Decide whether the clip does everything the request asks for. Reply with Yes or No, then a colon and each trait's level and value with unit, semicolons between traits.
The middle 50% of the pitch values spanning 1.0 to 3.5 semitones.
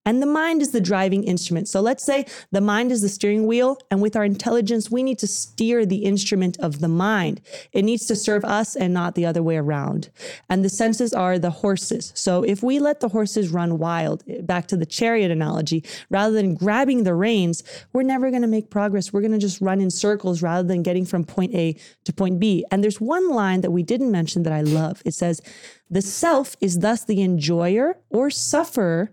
No: average, 4.3 semitones